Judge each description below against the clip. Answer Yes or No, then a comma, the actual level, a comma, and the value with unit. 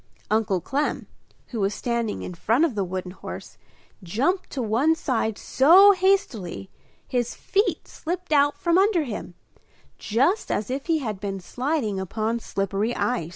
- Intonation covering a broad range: Yes, wide, 7.7 semitones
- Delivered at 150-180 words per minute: Yes, average, 155 wpm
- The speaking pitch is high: Yes, high, 240 Hz